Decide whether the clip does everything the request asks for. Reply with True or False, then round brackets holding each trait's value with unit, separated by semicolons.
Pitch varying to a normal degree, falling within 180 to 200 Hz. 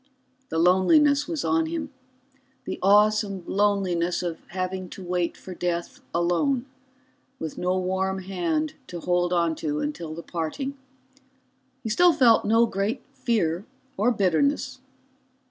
True (4.9 semitones; 190 Hz)